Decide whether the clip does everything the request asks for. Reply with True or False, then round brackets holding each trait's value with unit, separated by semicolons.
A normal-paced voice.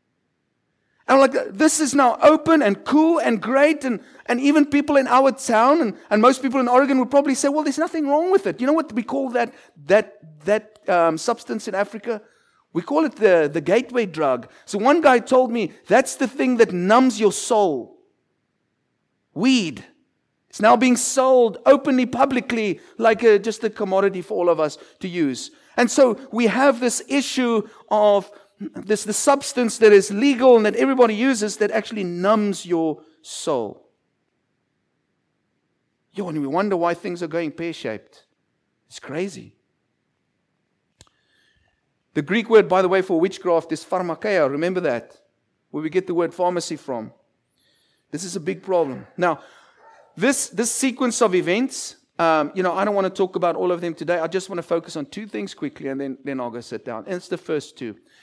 True (180 wpm)